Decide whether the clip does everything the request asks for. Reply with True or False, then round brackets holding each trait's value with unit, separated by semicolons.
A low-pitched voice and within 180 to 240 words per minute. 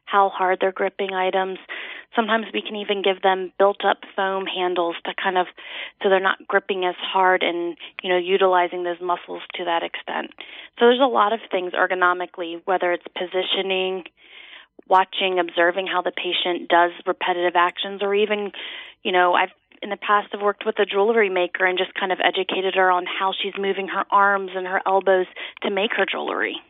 False (190 Hz; 185 wpm)